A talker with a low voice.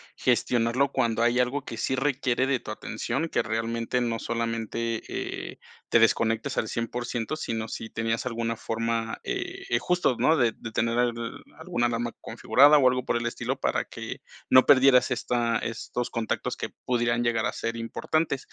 Yes: low, 120 Hz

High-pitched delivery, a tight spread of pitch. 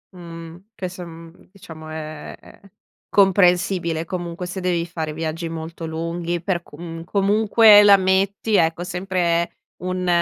No: medium, 175 Hz; narrow, 2.3 semitones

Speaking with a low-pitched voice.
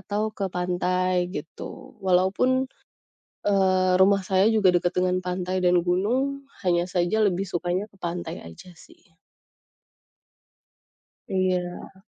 No: medium, 185 Hz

